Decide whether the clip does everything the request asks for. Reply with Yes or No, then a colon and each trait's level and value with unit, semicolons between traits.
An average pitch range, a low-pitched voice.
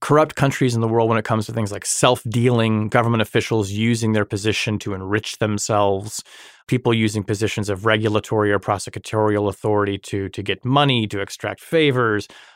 No: narrow, 2.0 semitones; low, 110 Hz